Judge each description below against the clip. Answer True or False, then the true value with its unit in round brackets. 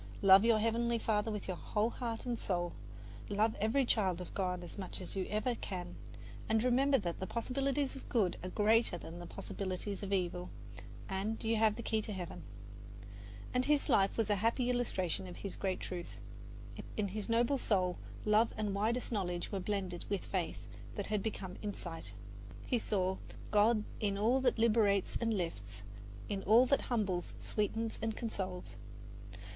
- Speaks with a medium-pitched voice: False (210 Hz)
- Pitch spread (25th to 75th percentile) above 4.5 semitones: False (3.5 semitones)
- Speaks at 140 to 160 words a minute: False (175 wpm)